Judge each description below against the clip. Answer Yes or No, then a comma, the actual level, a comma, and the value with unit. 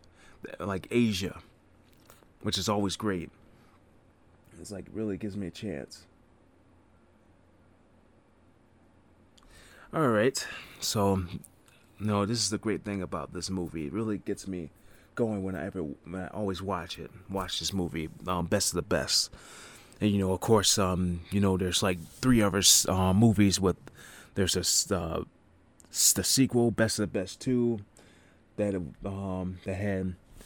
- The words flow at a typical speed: Yes, average, 150 wpm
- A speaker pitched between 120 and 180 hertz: No, very low, 95 Hz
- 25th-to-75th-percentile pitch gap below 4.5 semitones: Yes, average, 2.9 semitones